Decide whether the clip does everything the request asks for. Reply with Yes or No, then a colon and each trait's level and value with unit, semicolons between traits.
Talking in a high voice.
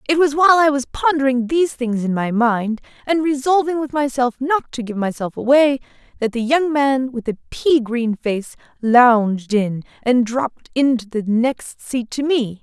Yes: very high, 255 Hz